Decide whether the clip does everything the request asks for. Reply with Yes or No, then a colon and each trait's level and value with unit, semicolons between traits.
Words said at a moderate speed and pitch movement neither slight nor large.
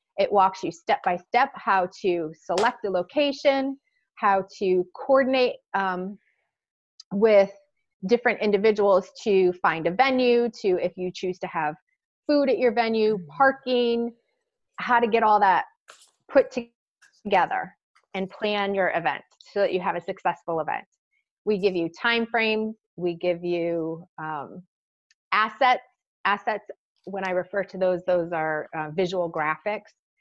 Yes: average, 145 wpm; average, 4.8 semitones